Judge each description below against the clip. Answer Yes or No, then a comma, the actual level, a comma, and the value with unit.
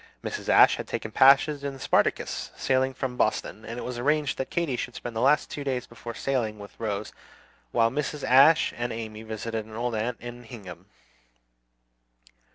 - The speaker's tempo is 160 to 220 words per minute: Yes, average, 180 wpm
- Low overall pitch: Yes, low, 120 Hz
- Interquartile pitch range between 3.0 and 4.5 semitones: Yes, average, 3.3 semitones